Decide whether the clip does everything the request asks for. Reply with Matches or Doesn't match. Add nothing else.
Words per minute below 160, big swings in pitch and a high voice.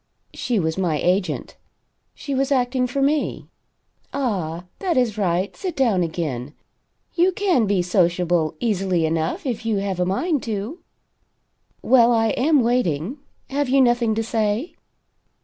Matches